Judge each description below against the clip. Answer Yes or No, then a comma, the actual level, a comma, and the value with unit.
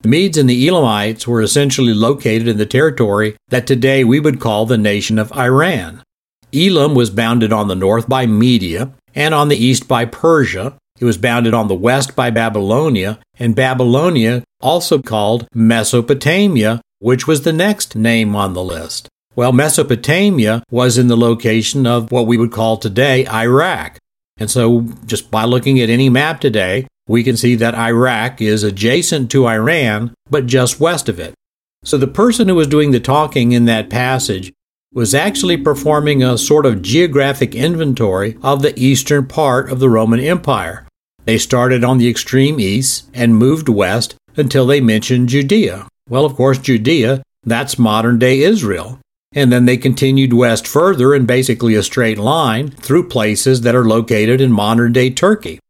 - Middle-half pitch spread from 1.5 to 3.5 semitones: Yes, average, 3.1 semitones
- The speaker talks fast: No, average, 170 wpm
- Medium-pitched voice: No, low, 125 Hz